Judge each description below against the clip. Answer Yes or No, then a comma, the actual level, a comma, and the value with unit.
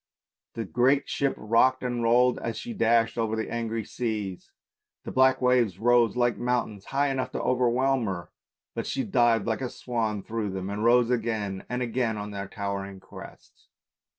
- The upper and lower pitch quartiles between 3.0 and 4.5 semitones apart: No, narrow, 2.6 semitones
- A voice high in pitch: No, low, 115 Hz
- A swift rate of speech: No, average, 175 wpm